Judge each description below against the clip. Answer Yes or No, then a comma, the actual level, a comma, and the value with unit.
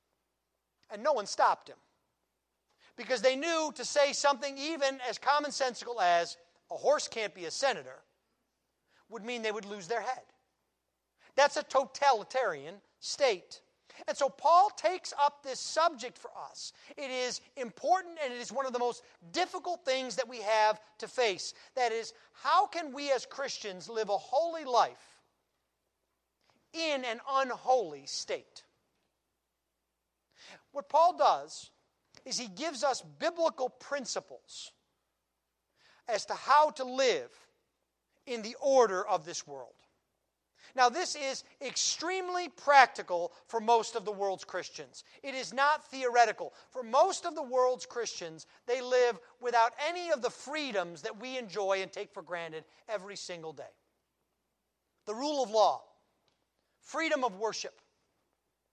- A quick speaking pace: No, average, 140 wpm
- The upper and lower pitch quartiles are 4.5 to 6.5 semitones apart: Yes, wide, 5.4 semitones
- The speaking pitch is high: Yes, very high, 255 Hz